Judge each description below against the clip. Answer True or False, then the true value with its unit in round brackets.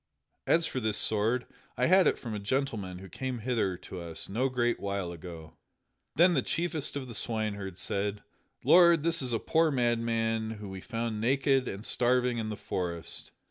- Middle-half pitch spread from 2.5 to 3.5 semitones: False (4.6 semitones)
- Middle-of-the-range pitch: False (115 Hz)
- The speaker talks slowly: False (180 wpm)